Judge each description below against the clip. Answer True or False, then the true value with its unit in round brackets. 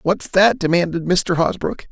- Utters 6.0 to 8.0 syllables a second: False (4.5 syllables/s)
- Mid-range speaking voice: True (170 Hz)